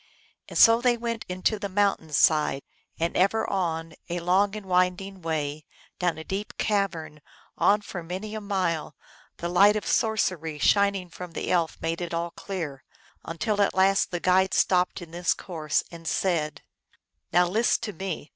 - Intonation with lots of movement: No, average, 3.3 semitones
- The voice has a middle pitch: Yes, medium, 180 Hz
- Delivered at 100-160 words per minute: No, average, 175 wpm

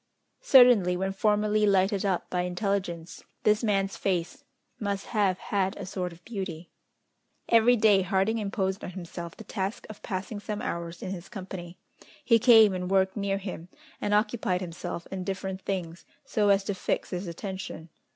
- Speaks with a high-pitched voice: Yes, high, 195 Hz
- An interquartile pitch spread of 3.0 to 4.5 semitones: No, narrow, 2.4 semitones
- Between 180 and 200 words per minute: No, average, 165 wpm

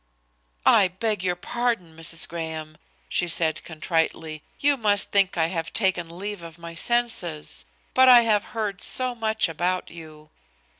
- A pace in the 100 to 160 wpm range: Yes, average, 150 wpm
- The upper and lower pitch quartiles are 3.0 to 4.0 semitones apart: No, average, 5.0 semitones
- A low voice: No, medium, 180 Hz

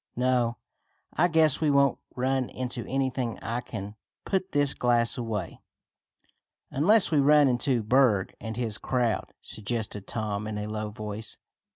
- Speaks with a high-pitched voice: No, low, 120 Hz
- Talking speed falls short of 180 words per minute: Yes, average, 150 wpm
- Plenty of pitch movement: No, average, 4.0 semitones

